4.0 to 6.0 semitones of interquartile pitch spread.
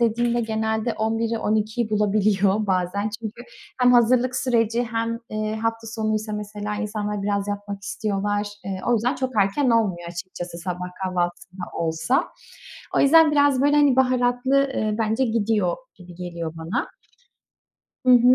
No: average, 3.2 semitones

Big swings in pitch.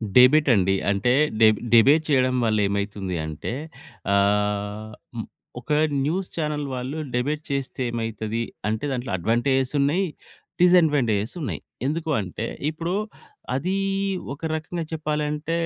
Yes: wide, 5.9 semitones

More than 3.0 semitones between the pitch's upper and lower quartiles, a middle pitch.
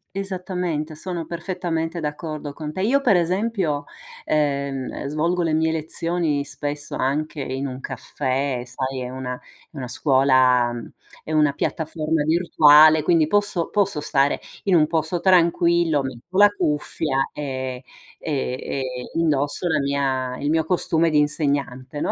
Yes: average, 3.4 semitones; medium, 155 Hz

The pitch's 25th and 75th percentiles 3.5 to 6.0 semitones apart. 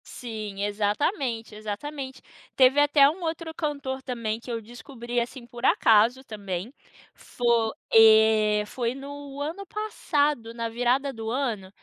Yes: average, 4.3 semitones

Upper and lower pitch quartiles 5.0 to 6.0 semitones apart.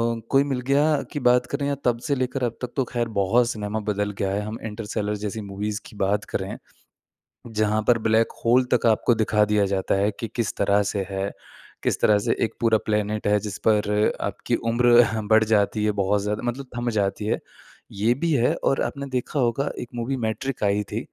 No: average, 2.8 semitones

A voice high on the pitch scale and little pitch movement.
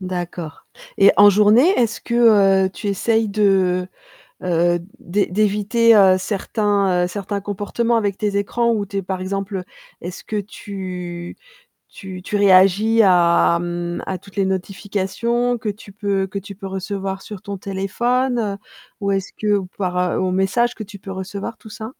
Yes: high, 200 Hz; narrow, 2.1 semitones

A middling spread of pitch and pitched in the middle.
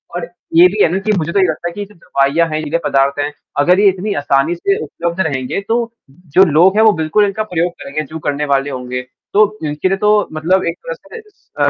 Yes: average, 4.8 semitones; medium, 170 Hz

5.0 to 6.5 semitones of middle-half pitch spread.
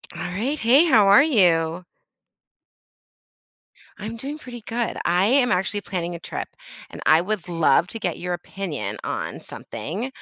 Yes: wide, 5.4 semitones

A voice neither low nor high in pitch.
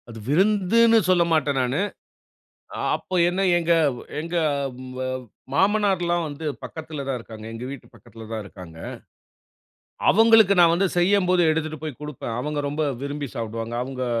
Yes: medium, 155 Hz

